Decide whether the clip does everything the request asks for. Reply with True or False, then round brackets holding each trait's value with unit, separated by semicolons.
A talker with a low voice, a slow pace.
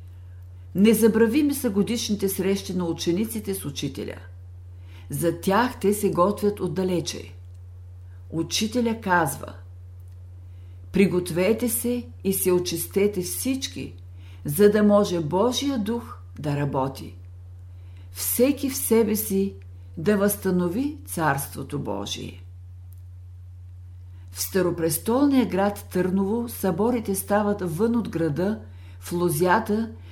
False (170 Hz; 95 wpm)